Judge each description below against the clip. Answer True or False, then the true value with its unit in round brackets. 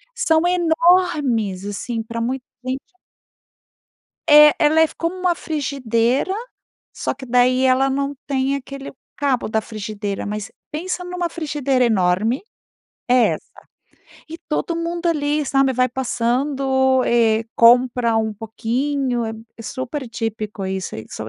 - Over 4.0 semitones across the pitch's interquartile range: True (4.6 semitones)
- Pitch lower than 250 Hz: False (260 Hz)